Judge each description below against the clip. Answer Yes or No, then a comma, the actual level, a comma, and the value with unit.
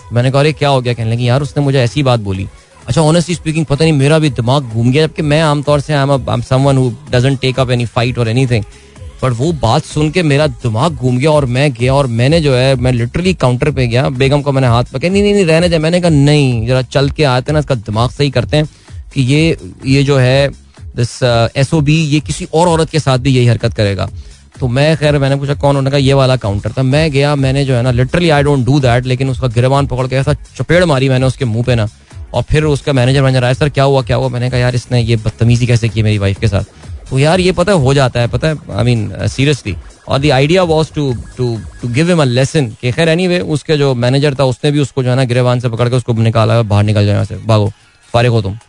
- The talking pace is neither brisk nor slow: No, fast, 255 wpm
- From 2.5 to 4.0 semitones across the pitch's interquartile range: Yes, average, 3.6 semitones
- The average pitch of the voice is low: Yes, low, 130 Hz